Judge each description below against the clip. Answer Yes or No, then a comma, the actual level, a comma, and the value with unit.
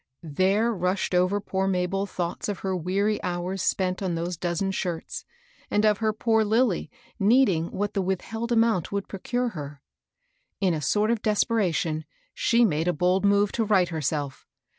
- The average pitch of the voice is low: No, high, 190 Hz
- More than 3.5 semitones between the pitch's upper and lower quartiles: No, average, 3.2 semitones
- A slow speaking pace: No, average, 165 wpm